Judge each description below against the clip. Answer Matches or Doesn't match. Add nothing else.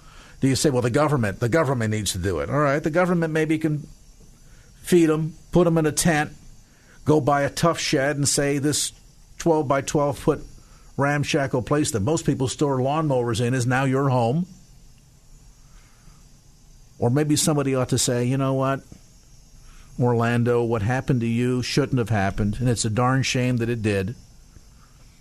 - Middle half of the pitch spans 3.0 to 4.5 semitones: Matches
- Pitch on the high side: Doesn't match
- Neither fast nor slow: Matches